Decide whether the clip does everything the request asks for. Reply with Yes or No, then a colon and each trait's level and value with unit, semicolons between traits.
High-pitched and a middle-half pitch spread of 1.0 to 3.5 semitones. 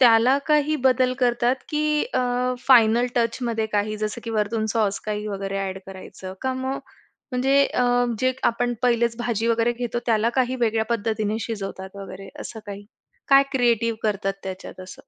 Yes: high, 230 Hz; average, 2.8 semitones